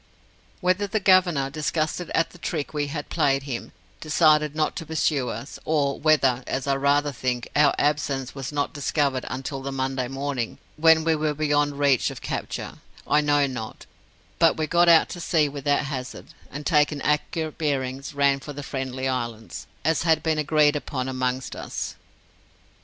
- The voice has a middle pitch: Yes, medium, 145 Hz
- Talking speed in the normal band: Yes, average, 170 wpm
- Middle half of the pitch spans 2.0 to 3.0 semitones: Yes, narrow, 2.5 semitones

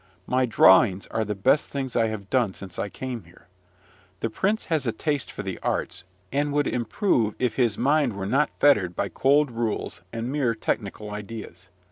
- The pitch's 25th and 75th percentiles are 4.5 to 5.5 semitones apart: Yes, average, 5.1 semitones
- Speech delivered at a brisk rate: No, average, 185 wpm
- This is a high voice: No, low, 115 Hz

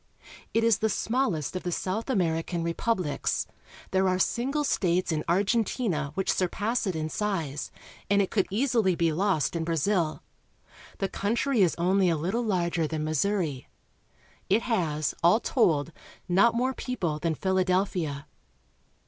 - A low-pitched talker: No, medium, 185 Hz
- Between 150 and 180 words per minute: No, average, 140 wpm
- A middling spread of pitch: Yes, average, 4.7 semitones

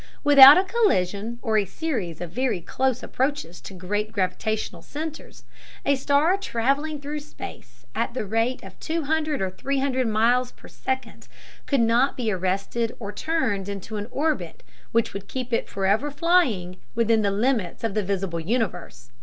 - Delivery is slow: No, average, 165 wpm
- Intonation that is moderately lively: No, wide, 6.0 semitones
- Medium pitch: No, high, 230 Hz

